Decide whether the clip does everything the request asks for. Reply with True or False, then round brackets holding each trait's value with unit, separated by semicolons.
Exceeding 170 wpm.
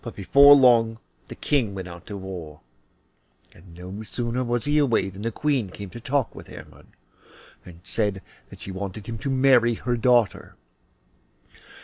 False (160 wpm)